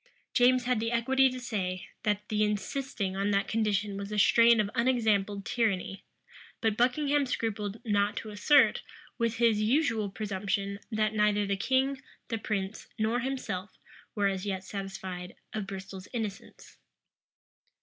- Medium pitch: No, high, 210 Hz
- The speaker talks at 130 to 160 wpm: Yes, average, 145 wpm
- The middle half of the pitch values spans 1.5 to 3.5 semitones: Yes, average, 2.9 semitones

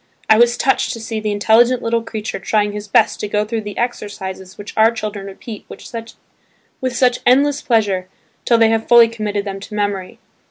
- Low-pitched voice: No, high, 220 Hz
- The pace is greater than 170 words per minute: Yes, average, 190 wpm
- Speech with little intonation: Yes, narrow, 2.2 semitones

